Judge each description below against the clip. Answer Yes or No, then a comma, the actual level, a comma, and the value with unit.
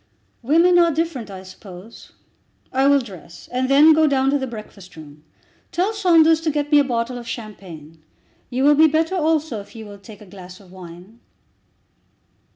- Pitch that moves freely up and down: Yes, wide, 7.9 semitones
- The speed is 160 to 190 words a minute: Yes, average, 180 wpm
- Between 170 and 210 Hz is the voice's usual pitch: No, very high, 250 Hz